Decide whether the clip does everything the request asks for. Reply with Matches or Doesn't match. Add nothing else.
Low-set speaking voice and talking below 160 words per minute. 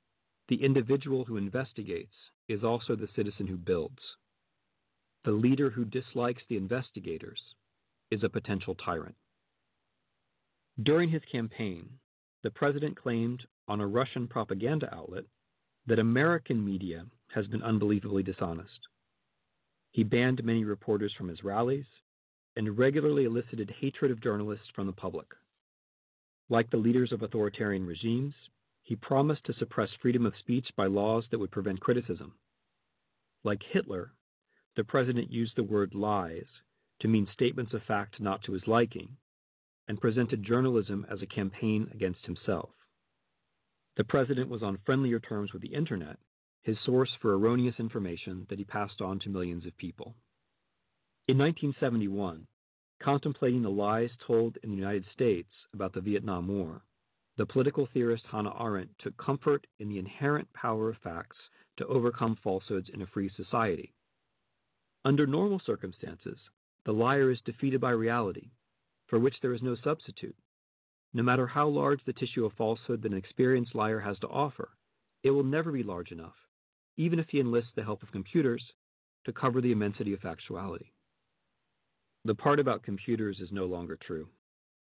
Matches